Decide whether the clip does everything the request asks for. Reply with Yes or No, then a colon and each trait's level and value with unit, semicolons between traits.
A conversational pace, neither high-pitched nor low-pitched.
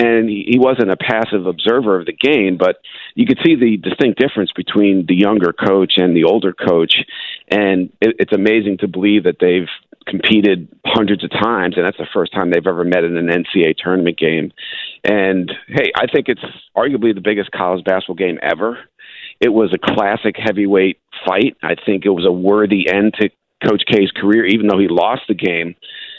No: average, 190 wpm; low, 100 Hz